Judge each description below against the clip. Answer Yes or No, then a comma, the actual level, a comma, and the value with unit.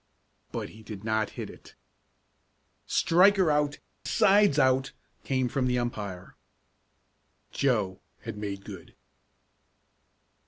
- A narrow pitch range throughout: No, wide, 5.6 semitones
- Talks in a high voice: No, low, 125 Hz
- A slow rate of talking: Yes, slow, 105 wpm